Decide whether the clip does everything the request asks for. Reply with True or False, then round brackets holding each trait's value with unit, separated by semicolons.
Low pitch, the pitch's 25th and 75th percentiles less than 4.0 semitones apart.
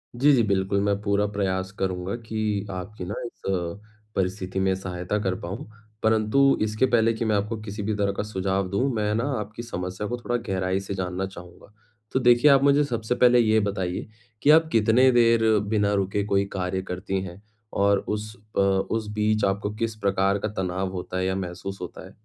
True (100 Hz; 2.8 semitones)